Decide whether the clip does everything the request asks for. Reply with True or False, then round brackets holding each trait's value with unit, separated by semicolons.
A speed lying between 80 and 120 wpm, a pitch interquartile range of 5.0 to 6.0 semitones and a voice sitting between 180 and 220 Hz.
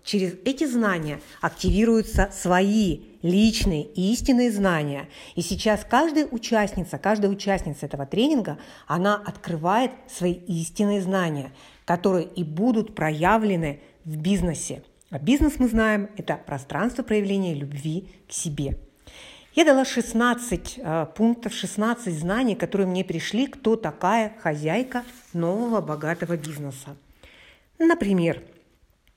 True (115 wpm; 5.3 semitones; 190 Hz)